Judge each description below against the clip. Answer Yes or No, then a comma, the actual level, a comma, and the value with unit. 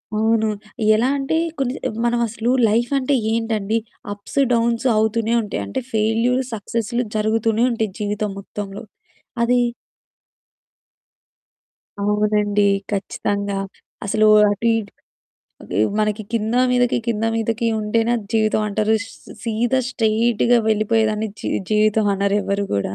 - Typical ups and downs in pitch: No, narrow, 1.8 semitones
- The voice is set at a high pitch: Yes, high, 220 Hz